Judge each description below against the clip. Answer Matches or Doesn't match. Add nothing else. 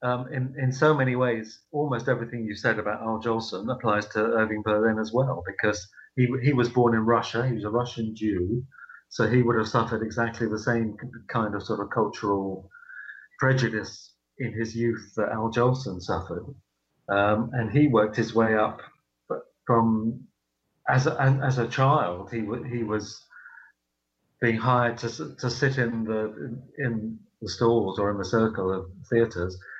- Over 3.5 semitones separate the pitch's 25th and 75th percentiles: Doesn't match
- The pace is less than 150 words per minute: Doesn't match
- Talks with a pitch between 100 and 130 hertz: Matches